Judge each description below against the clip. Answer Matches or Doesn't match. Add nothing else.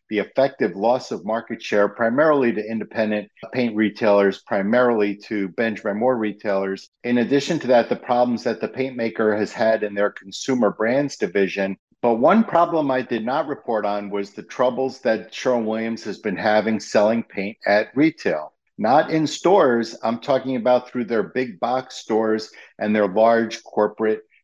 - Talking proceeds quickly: Doesn't match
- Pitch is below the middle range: Matches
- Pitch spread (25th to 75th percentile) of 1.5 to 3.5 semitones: Matches